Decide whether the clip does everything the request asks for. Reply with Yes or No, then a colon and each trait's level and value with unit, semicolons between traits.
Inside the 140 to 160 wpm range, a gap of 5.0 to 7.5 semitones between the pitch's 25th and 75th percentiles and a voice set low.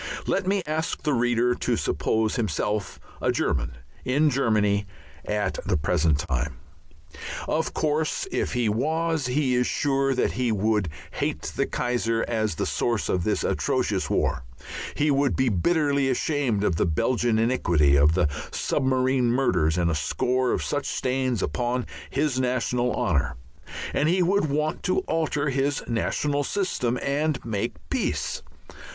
Yes: average, 150 wpm; wide, 5.4 semitones; low, 125 Hz